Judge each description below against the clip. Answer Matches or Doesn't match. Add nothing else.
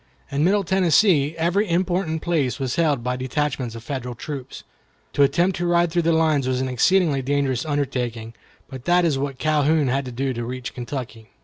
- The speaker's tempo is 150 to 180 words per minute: Doesn't match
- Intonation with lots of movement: Doesn't match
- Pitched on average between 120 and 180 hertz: Matches